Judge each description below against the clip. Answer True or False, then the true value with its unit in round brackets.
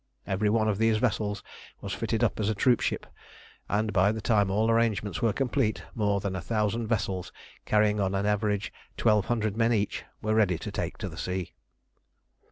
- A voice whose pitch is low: True (105 Hz)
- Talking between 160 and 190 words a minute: True (180 wpm)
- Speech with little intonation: True (1.9 semitones)